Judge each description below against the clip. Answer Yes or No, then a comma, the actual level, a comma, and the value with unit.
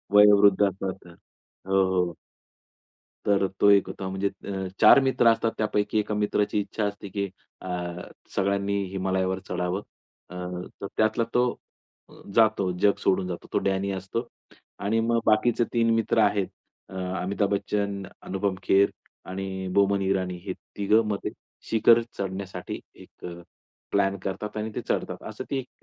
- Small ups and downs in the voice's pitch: Yes, narrow, 1.8 semitones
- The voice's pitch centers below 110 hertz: Yes, low, 100 Hz